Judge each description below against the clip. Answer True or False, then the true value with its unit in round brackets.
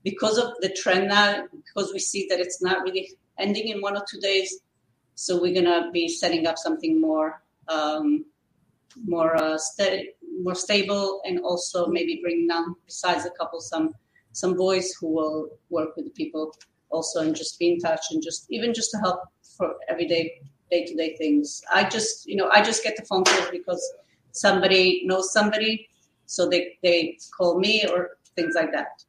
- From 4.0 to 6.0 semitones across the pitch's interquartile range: False (3.2 semitones)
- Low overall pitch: False (180 Hz)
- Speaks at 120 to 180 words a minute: False (190 wpm)